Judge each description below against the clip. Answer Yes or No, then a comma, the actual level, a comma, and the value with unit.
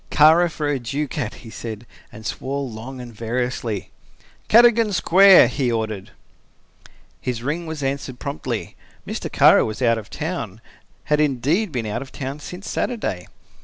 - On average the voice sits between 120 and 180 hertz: Yes, low, 135 Hz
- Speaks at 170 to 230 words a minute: No, average, 150 wpm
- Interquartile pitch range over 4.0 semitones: Yes, average, 4.9 semitones